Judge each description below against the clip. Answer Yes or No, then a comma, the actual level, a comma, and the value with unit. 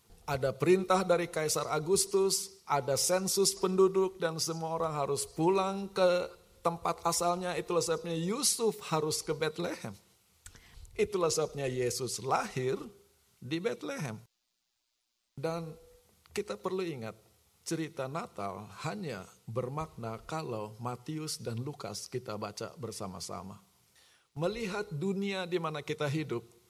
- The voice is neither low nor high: Yes, medium, 160 Hz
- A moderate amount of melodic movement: No, wide, 6.0 semitones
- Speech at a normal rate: Yes, average, 110 wpm